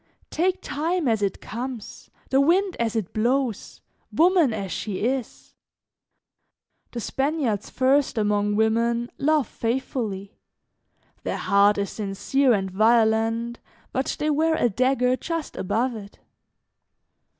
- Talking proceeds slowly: Yes, slow, 120 wpm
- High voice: Yes, high, 235 Hz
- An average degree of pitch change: Yes, average, 4.4 semitones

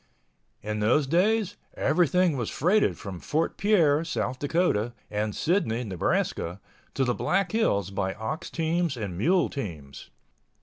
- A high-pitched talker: No, medium, 140 Hz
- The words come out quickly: No, slow, 135 wpm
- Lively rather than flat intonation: Yes, wide, 9.0 semitones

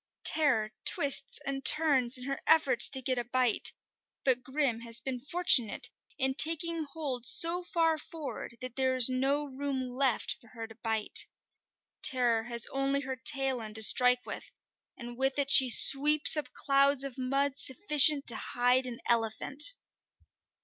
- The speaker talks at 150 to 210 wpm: Yes, average, 160 wpm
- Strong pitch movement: No, narrow, 2.5 semitones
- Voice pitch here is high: Yes, very high, 265 Hz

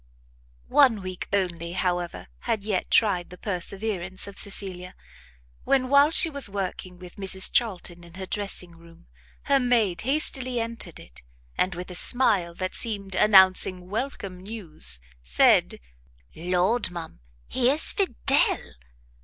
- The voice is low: No, high, 190 Hz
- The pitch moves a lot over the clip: No, average, 4.2 semitones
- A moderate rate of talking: No, slow, 130 wpm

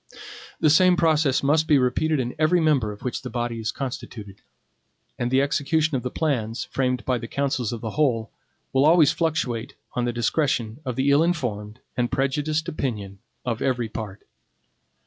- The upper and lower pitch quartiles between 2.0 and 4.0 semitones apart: No, average, 4.5 semitones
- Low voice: Yes, low, 130 Hz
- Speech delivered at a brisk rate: No, average, 175 wpm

